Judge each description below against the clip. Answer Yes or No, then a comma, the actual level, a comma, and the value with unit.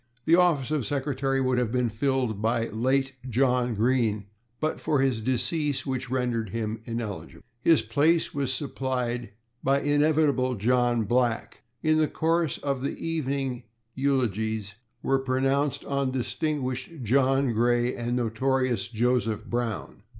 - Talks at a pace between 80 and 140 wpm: Yes, slow, 135 wpm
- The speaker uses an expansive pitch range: No, average, 2.7 semitones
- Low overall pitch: Yes, low, 130 Hz